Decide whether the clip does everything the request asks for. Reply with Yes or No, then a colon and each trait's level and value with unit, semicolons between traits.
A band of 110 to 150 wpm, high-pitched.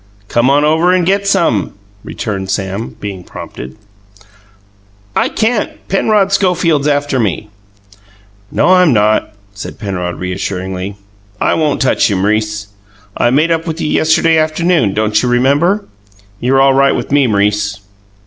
No: average, 140 wpm; low, 130 Hz